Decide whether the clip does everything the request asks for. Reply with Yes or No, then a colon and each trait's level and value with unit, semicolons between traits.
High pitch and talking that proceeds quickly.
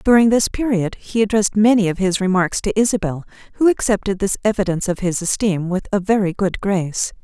No: high, 200 Hz; average, 190 wpm